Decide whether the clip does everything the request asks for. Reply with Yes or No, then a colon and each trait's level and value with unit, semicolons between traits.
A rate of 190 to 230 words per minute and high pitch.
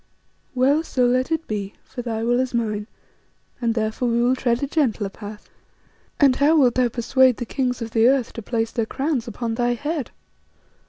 Yes: average, 195 wpm; high, 245 Hz